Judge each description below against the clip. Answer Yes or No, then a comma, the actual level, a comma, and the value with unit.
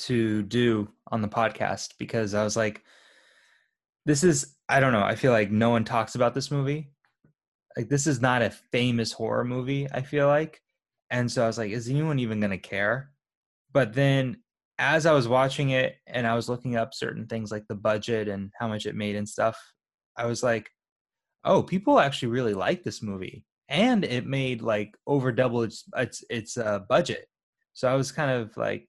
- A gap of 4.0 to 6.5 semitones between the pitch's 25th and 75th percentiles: No, average, 3.6 semitones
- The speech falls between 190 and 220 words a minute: Yes, average, 200 wpm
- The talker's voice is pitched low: Yes, low, 120 Hz